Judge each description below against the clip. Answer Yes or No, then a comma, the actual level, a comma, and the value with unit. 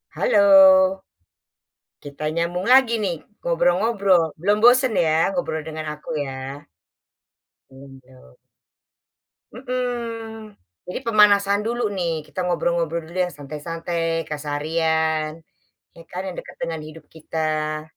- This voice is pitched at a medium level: Yes, medium, 170 Hz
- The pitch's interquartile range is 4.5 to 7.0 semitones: Yes, average, 4.9 semitones